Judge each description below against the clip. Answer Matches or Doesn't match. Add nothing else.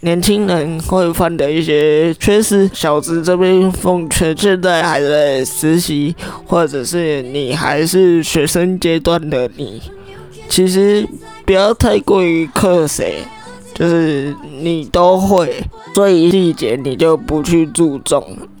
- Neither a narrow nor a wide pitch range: Matches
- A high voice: Doesn't match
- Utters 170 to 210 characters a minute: Matches